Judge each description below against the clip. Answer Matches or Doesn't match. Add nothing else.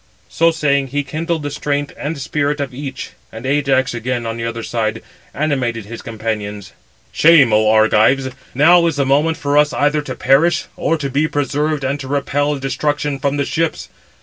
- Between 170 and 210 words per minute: Matches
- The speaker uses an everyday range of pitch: Matches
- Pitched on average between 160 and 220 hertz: Doesn't match